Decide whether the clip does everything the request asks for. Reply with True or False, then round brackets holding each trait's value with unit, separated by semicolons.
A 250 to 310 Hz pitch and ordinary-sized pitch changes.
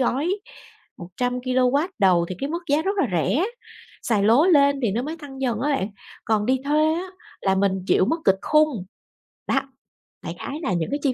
False (260 Hz; 6.4 semitones)